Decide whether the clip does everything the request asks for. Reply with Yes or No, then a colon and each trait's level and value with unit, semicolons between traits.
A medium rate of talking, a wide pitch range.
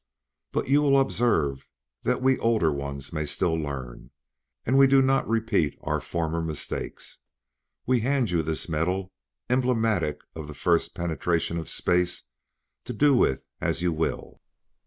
Yes: average, 150 wpm; wide, 7.8 semitones